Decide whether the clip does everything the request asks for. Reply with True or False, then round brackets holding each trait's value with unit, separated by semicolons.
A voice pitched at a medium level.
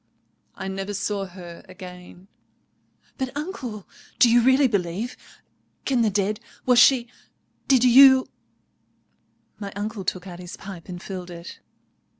False (205 Hz)